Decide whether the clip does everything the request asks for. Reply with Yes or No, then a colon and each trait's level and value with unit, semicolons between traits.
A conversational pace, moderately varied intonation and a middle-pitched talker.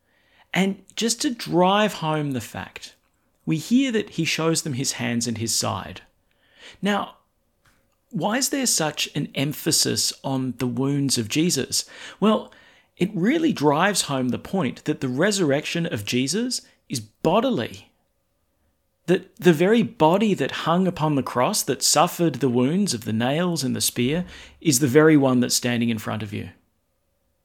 No: average, 160 wpm; wide, 7.2 semitones; medium, 150 Hz